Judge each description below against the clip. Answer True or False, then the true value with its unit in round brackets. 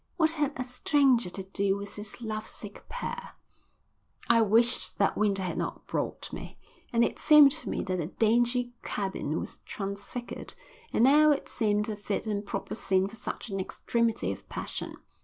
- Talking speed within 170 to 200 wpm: True (175 wpm)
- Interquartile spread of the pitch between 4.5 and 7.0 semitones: False (3.9 semitones)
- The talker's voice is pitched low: False (220 Hz)